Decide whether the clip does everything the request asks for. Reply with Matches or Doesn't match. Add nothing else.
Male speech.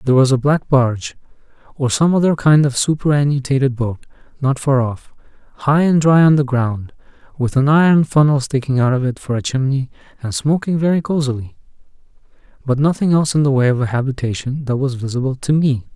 Matches